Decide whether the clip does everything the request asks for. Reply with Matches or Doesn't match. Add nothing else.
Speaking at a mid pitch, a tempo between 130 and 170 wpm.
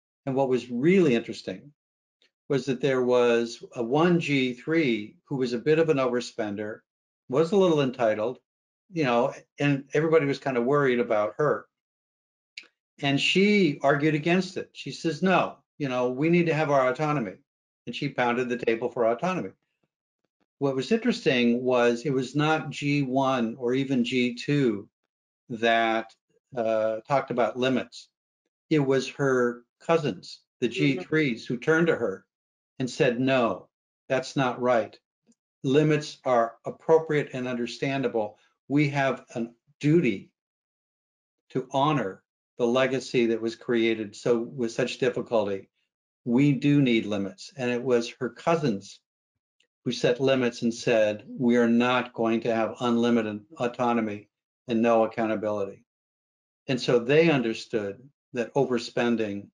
Doesn't match